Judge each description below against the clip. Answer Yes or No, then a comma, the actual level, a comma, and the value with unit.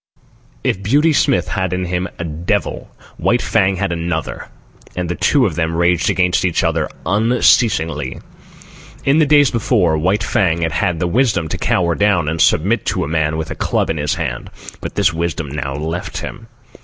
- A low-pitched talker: Yes, very low, 90 Hz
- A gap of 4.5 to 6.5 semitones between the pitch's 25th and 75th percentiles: No, average, 3.8 semitones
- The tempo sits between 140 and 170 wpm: No, average, 185 wpm